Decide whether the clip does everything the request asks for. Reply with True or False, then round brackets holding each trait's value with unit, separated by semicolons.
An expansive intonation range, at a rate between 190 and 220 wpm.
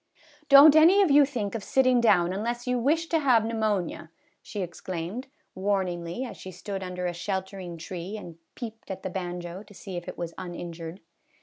True (5.7 semitones; 195 wpm)